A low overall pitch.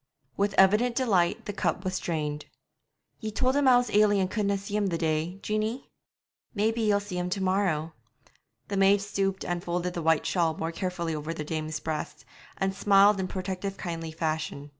No: high, 190 Hz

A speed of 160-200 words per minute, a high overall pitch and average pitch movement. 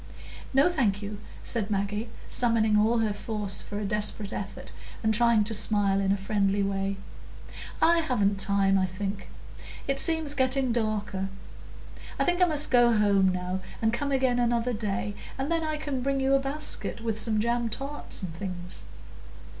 Yes: average, 170 wpm; high, 220 Hz; average, 4.7 semitones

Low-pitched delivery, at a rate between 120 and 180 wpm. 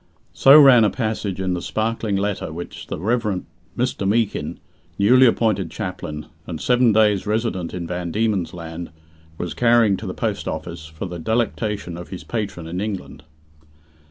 Yes: low, 100 Hz; average, 160 wpm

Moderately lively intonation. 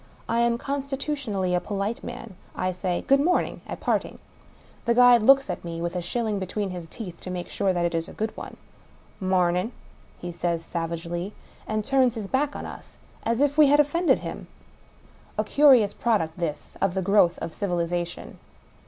No: wide, 5.8 semitones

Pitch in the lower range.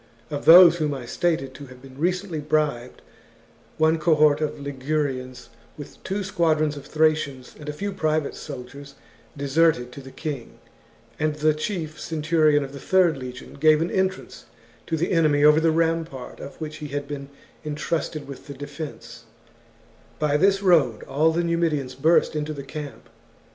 No: medium, 150 Hz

